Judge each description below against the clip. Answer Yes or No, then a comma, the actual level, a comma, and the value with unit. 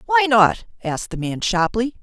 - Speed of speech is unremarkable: Yes, average, 180 wpm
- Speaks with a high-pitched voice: Yes, high, 220 Hz